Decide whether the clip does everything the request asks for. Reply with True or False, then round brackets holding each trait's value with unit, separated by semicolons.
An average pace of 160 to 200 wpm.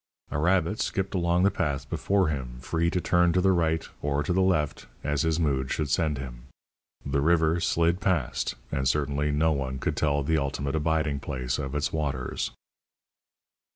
True (180 wpm)